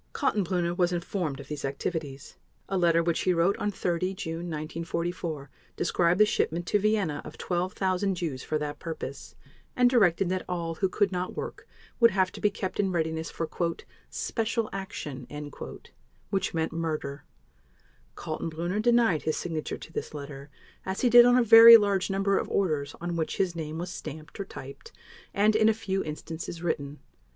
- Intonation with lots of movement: No, average, 3.7 semitones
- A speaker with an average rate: Yes, average, 170 wpm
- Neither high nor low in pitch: Yes, medium, 175 Hz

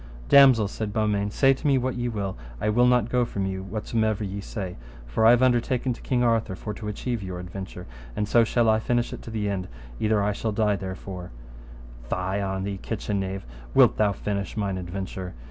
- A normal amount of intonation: Yes, average, 3.2 semitones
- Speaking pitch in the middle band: No, low, 105 Hz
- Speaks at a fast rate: Yes, fast, 210 wpm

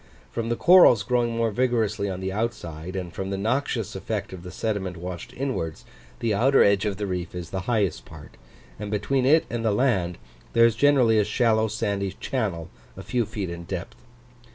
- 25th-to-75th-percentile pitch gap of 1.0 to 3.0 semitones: No, average, 3.7 semitones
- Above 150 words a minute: Yes, average, 195 wpm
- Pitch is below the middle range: Yes, low, 105 Hz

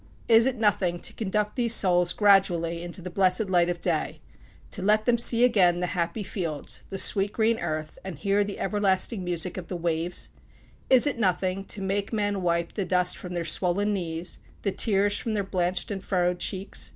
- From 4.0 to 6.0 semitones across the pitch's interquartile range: No, average, 2.8 semitones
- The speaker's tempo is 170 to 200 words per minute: Yes, average, 195 wpm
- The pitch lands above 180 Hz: Yes, high, 190 Hz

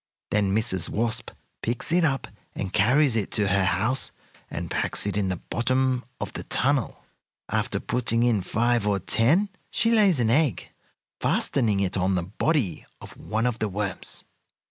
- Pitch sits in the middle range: No, low, 115 Hz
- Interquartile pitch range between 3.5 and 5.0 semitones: Yes, average, 4.7 semitones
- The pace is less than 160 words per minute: No, average, 165 wpm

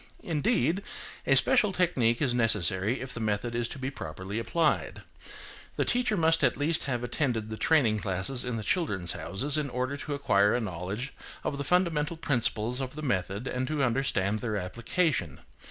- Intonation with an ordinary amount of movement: No, wide, 5.7 semitones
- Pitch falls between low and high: No, low, 125 Hz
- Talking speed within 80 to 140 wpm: No, average, 175 wpm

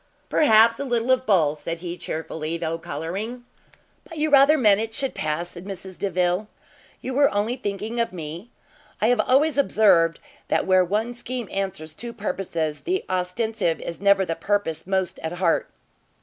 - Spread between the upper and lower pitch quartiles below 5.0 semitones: No, wide, 5.6 semitones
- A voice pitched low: No, high, 195 Hz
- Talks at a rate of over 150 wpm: Yes, average, 170 wpm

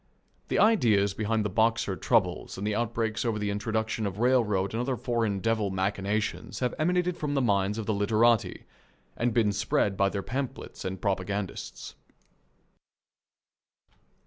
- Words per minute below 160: Yes, average, 145 wpm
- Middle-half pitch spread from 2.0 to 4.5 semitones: Yes, average, 2.8 semitones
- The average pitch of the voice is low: Yes, low, 110 Hz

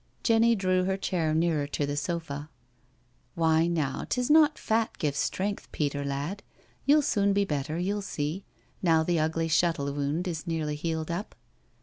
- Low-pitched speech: No, medium, 165 Hz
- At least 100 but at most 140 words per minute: No, average, 165 wpm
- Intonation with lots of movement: No, average, 4.6 semitones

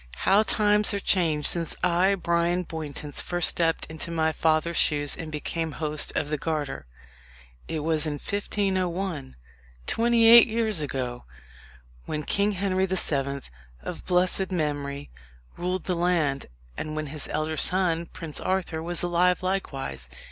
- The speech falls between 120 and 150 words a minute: Yes, average, 145 wpm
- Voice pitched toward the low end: No, medium, 170 Hz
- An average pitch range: Yes, average, 3.5 semitones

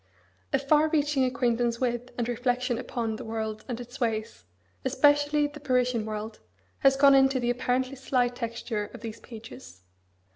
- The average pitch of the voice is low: No, high, 245 Hz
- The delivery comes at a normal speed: Yes, average, 155 wpm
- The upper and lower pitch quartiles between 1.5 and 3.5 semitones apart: Yes, average, 2.8 semitones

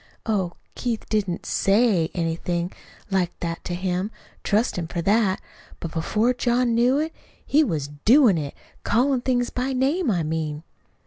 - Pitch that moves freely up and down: Yes, wide, 6.2 semitones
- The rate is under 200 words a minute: Yes, average, 150 wpm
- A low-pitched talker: No, high, 205 Hz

